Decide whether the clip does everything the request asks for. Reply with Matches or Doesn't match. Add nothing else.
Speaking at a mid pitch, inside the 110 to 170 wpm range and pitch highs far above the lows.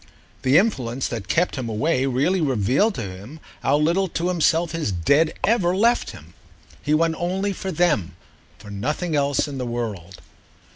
Matches